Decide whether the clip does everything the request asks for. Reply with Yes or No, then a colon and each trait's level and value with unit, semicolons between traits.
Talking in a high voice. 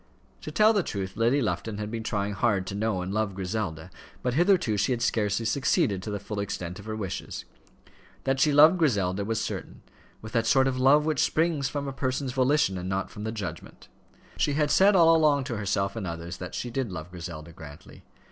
No: low, 110 Hz